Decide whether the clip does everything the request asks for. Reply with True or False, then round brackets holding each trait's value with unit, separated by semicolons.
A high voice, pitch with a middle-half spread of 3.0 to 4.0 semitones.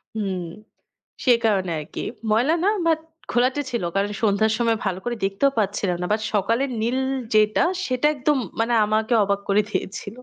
True (220 Hz; 3.5 semitones)